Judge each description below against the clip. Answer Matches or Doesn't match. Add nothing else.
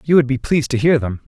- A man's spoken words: Matches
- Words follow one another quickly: Matches